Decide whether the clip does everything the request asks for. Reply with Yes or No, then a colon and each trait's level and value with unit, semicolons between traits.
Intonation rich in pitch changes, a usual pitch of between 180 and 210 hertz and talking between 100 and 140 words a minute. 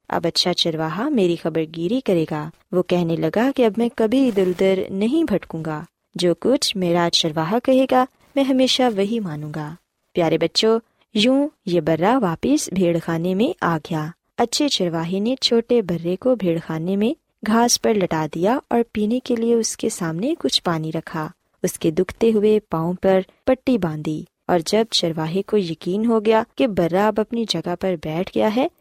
No: wide, 5.7 semitones; high, 190 Hz; average, 185 wpm